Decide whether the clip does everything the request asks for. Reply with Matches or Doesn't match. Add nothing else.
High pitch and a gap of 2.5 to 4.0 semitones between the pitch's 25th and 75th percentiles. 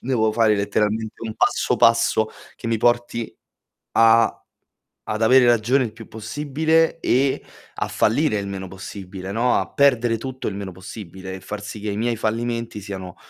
Doesn't match